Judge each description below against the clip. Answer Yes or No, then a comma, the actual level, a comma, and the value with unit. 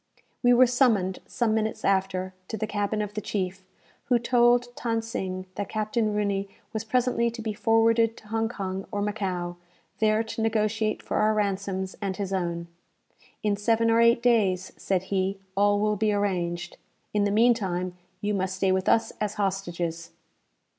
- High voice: Yes, high, 210 Hz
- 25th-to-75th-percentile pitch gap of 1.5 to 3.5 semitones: Yes, average, 2.9 semitones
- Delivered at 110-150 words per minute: No, average, 175 wpm